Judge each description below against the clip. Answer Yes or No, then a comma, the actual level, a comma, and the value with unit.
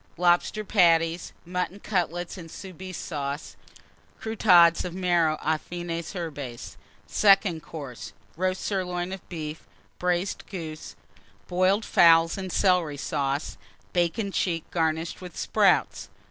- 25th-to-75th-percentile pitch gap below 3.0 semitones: Yes, narrow, 2.4 semitones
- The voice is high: No, medium, 175 Hz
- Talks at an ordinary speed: No, slow, 115 wpm